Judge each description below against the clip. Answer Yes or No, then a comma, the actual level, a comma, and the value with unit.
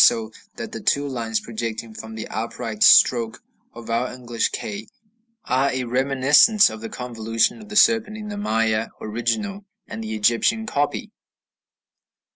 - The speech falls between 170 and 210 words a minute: No, average, 150 wpm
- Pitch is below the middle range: Yes, low, 120 Hz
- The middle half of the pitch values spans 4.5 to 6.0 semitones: No, average, 4.0 semitones